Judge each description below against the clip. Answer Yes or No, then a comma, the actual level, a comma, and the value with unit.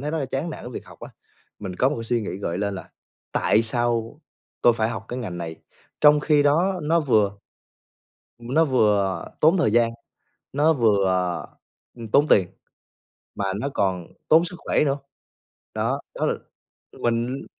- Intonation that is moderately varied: No, wide, 6.3 semitones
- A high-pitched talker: No, low, 120 Hz